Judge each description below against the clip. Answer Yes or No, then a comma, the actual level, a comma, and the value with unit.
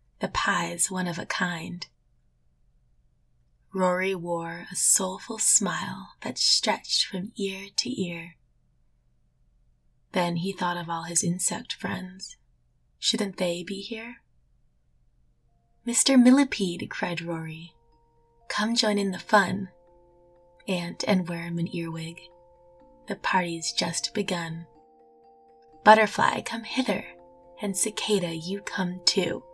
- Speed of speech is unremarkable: No, slow, 110 wpm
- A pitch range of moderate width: Yes, average, 3.9 semitones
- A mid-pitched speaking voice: Yes, medium, 175 Hz